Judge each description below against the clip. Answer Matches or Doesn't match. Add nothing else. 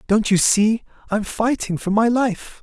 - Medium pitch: Doesn't match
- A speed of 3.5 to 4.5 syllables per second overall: Matches